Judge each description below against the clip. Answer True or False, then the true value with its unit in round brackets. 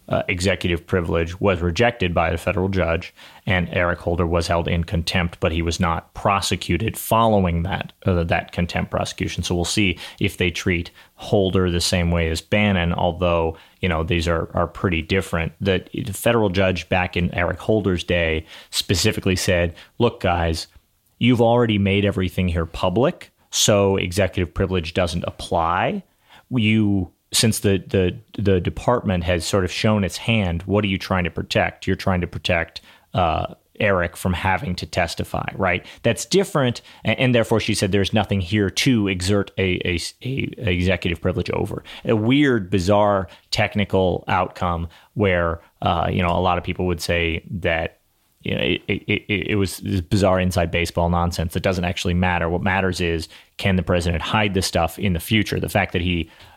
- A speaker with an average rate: True (175 wpm)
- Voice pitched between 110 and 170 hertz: False (95 Hz)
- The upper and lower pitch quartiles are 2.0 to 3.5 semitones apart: True (2.9 semitones)